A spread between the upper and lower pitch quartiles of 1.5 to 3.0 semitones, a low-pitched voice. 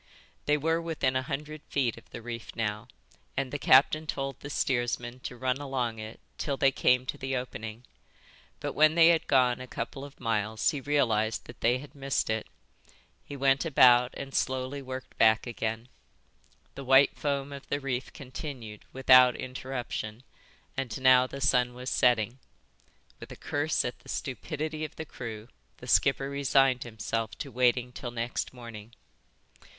Yes: narrow, 2.4 semitones; low, 130 Hz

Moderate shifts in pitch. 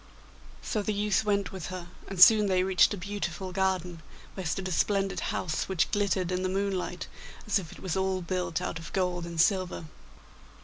No: narrow, 1.8 semitones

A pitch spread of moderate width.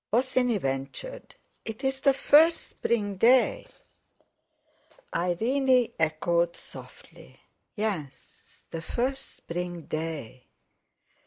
No: wide, 7.8 semitones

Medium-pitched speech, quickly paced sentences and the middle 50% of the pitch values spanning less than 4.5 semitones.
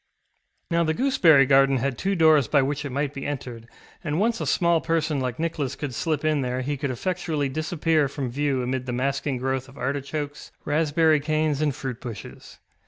No: medium, 145 Hz; average, 195 wpm; average, 2.9 semitones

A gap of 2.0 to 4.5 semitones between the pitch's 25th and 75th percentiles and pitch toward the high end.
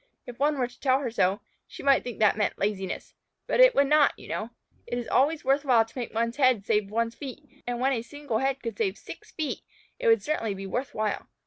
Yes: average, 4.0 semitones; high, 245 Hz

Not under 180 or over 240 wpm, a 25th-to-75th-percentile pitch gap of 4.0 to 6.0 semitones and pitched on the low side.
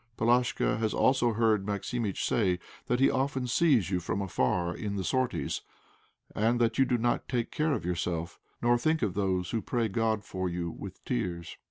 Yes: average, 185 wpm; average, 4.8 semitones; low, 110 Hz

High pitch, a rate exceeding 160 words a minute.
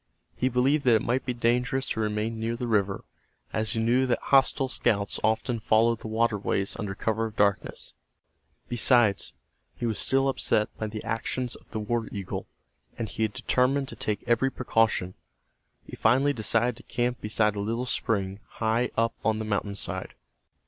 No: low, 115 Hz; average, 170 wpm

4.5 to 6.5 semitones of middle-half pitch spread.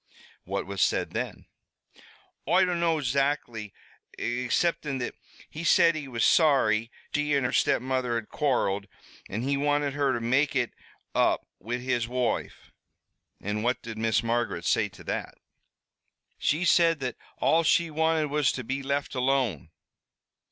No: average, 4.0 semitones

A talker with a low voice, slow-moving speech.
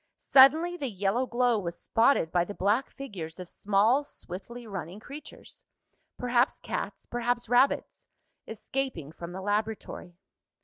No: high, 220 Hz; slow, 130 wpm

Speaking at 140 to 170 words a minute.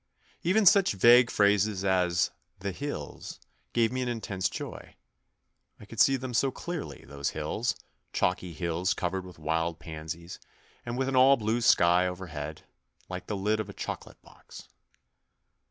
Yes: average, 165 wpm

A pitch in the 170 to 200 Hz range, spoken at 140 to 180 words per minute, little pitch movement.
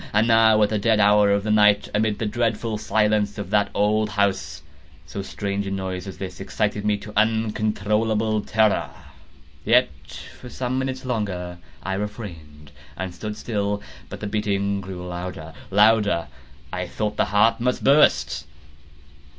No: low, 105 Hz; average, 155 wpm; narrow, 1.9 semitones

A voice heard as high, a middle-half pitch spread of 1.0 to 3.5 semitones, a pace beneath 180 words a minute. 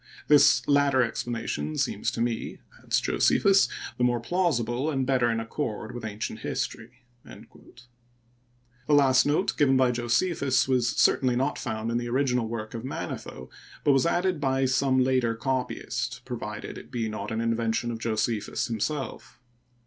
No: low, 125 Hz; average, 2.7 semitones; average, 155 wpm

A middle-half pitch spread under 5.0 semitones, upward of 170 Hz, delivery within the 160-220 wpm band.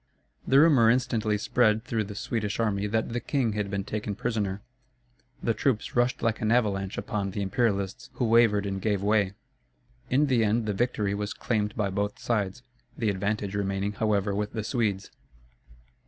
No: narrow, 2.5 semitones; low, 105 Hz; average, 170 wpm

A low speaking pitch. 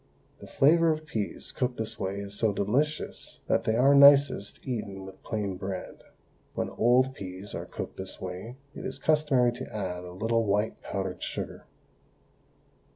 Yes: low, 110 Hz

